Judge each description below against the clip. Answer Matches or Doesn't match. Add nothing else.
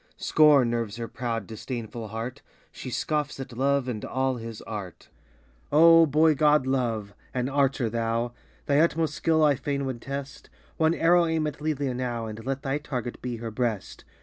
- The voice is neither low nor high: Doesn't match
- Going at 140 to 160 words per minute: Doesn't match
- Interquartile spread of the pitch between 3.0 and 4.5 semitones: Matches